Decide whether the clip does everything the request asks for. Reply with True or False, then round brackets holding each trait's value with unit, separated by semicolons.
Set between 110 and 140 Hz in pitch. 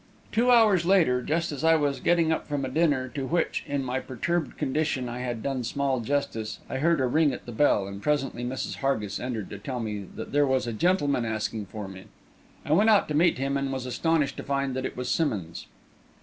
True (135 Hz)